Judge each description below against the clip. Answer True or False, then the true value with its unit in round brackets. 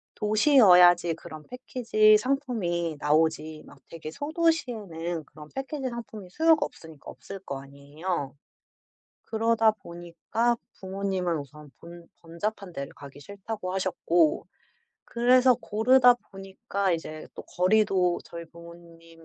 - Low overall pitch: False (185 Hz)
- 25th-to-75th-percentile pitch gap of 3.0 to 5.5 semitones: True (5.2 semitones)